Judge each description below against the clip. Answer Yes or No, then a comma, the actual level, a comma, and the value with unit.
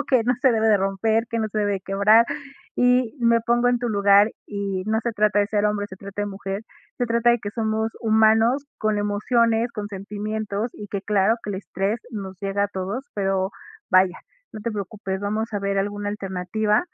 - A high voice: Yes, high, 210 Hz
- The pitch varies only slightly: Yes, narrow, 2.1 semitones